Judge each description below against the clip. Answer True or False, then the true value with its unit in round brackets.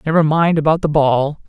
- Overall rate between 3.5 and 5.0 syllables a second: False (5.3 syllables/s)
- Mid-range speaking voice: True (155 Hz)